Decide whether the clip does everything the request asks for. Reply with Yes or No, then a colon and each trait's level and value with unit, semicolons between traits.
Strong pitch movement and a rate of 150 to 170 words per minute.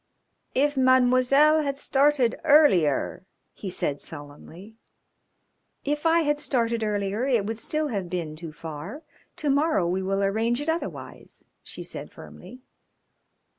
No: wide, 7.4 semitones; slow, 135 wpm